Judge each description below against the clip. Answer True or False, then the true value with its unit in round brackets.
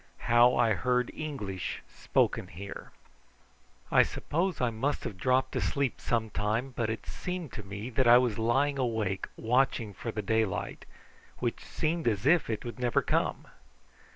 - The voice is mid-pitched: False (120 Hz)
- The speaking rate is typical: True (155 wpm)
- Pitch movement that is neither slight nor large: True (3.4 semitones)